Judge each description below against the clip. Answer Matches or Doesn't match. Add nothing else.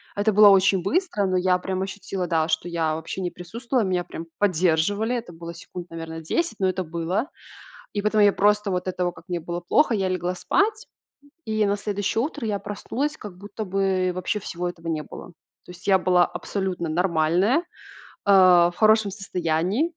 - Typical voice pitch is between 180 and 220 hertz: Matches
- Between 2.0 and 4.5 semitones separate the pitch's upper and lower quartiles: Matches